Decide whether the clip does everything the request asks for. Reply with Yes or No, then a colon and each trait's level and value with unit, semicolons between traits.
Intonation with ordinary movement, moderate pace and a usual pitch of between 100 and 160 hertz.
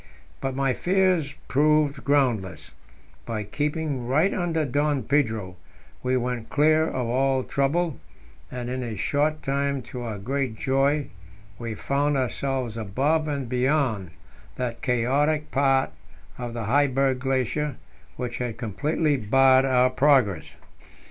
No: average, 3.0 semitones; slow, 130 wpm; low, 135 Hz